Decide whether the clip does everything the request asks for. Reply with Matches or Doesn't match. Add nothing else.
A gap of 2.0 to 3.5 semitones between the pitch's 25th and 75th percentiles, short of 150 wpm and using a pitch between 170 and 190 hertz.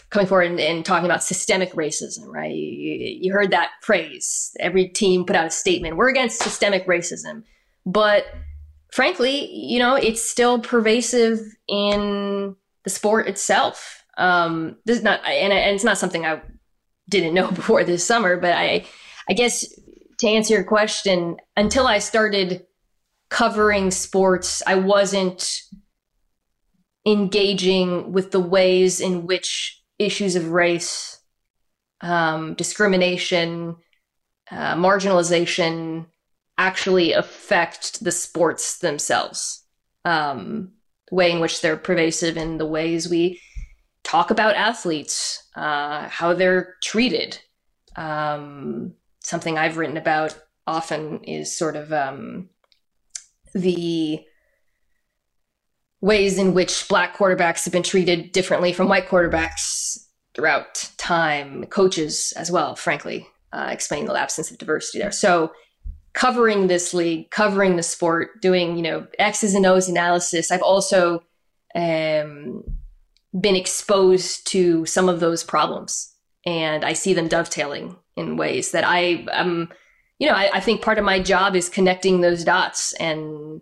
Matches